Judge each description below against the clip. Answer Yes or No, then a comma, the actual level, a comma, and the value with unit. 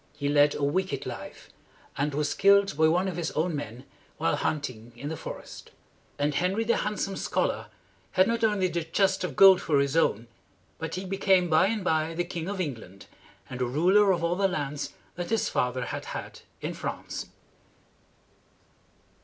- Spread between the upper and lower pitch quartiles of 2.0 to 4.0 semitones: No, average, 4.9 semitones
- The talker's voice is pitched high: No, medium, 165 Hz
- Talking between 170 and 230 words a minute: Yes, average, 180 wpm